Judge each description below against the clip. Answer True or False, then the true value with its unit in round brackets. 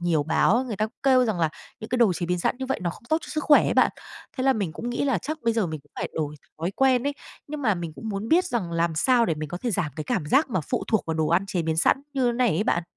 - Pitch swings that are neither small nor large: False (7.1 semitones)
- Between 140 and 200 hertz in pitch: False (210 Hz)